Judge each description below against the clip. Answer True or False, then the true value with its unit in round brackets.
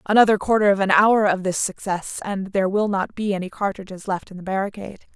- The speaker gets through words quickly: True (220 wpm)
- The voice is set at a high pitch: True (195 Hz)